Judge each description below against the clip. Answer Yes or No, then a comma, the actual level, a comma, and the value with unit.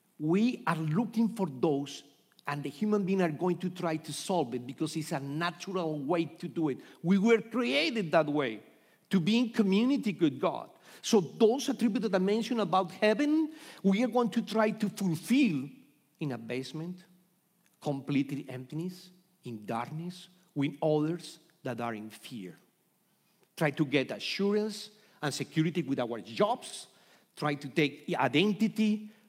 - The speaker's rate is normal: Yes, average, 155 wpm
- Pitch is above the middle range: No, medium, 180 Hz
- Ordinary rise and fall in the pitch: No, wide, 6.0 semitones